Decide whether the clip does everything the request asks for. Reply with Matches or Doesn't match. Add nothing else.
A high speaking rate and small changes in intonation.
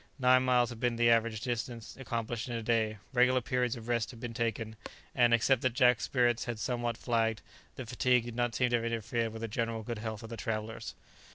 Matches